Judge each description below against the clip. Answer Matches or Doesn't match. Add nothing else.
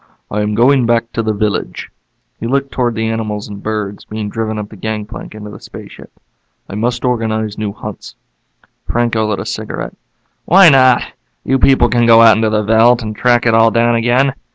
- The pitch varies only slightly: Matches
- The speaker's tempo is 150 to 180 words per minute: Doesn't match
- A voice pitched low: Matches